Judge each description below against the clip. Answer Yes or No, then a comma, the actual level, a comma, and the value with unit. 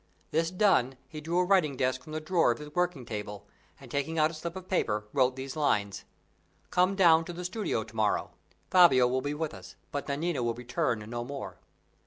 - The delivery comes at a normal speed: No, fast, 210 wpm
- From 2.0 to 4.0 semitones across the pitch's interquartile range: No, wide, 5.5 semitones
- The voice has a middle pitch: Yes, medium, 145 Hz